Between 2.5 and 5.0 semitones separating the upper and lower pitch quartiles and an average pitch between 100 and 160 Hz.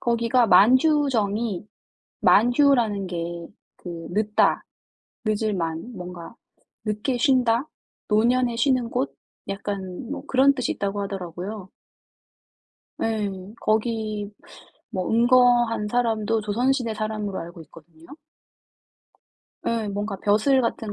No: average, 3.5 semitones; high, 215 Hz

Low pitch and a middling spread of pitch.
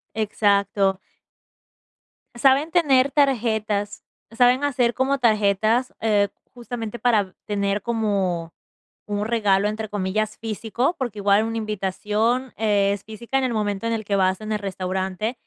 No: high, 215 Hz; average, 3.0 semitones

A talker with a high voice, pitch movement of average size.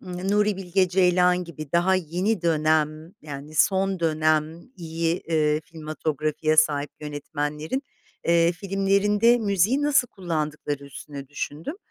No: medium, 165 Hz; average, 3.7 semitones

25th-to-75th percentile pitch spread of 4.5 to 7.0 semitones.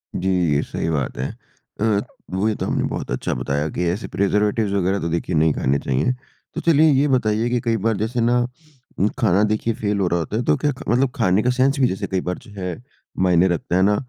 Yes: average, 5.1 semitones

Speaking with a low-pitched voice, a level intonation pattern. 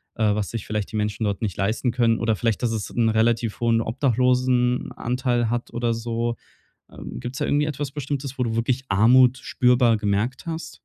Yes: low, 120 Hz; narrow, 2.2 semitones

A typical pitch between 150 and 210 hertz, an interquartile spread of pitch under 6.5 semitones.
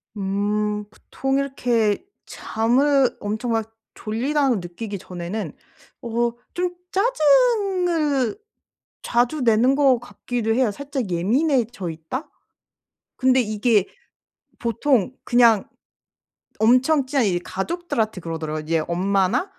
No: high, 235 Hz; average, 5.1 semitones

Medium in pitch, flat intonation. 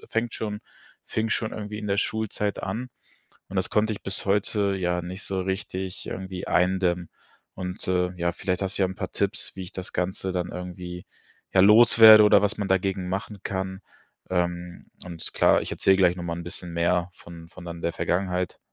No: very low, 95 Hz; narrow, 2.1 semitones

